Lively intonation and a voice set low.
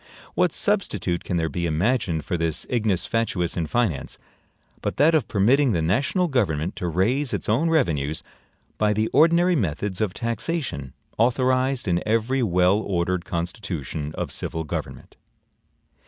Yes: wide, 6.9 semitones; low, 105 Hz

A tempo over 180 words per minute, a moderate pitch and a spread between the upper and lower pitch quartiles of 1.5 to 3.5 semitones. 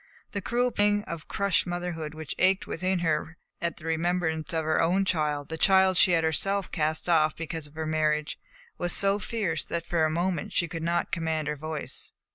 Yes: average, 200 wpm; medium, 165 Hz; average, 2.8 semitones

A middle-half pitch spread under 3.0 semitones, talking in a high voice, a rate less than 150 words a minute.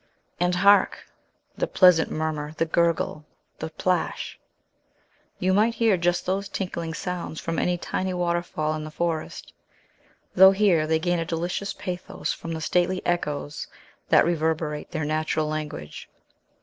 No: narrow, 2.5 semitones; medium, 170 Hz; average, 140 wpm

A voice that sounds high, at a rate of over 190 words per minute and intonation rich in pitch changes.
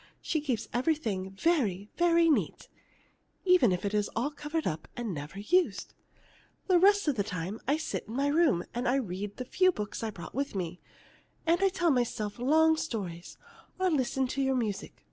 No: very high, 255 Hz; average, 180 wpm; wide, 7.8 semitones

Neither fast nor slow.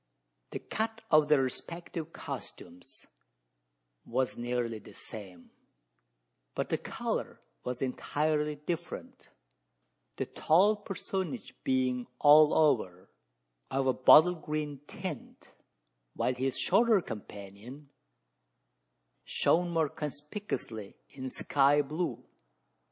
No: slow, 95 wpm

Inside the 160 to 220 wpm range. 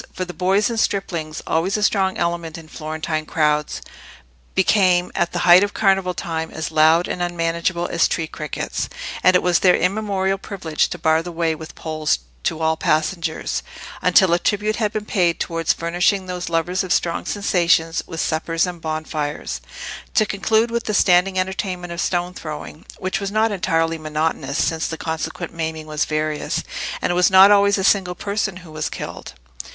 Yes: average, 180 wpm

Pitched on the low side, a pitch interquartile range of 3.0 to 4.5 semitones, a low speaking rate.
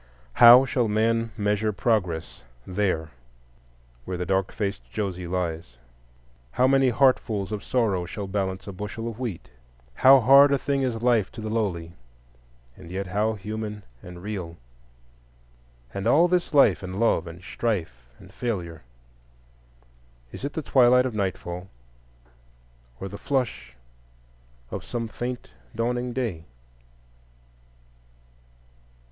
No: low, 105 Hz; wide, 5.4 semitones; slow, 125 wpm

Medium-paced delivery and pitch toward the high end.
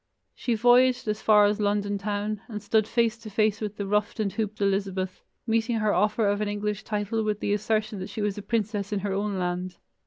No: fast, 220 wpm; high, 210 Hz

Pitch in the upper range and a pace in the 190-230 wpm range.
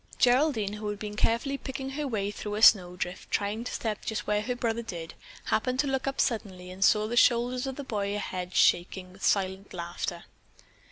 Yes: high, 210 Hz; average, 200 wpm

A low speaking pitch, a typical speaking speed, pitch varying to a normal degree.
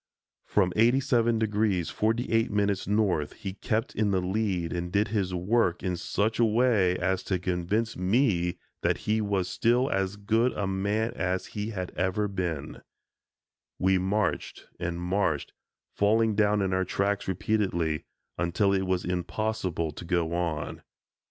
Yes: very low, 95 Hz; average, 145 wpm; average, 3.3 semitones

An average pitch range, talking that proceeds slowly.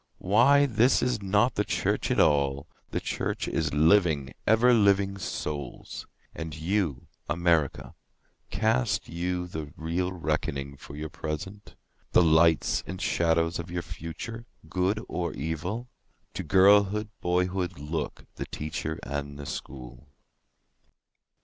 Yes: average, 4.6 semitones; slow, 105 wpm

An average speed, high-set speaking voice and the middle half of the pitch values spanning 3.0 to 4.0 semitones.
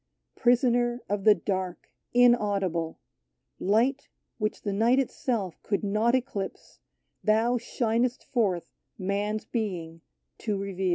No: slow, 115 wpm; high, 215 Hz; average, 3.6 semitones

